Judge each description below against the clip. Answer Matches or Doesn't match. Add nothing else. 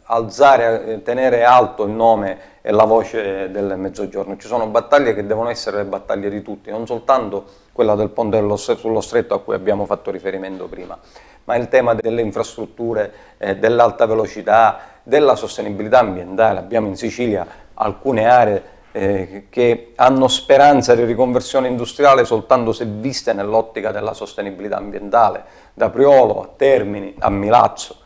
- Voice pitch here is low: Matches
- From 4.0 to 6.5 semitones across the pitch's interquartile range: Doesn't match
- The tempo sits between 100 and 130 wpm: Doesn't match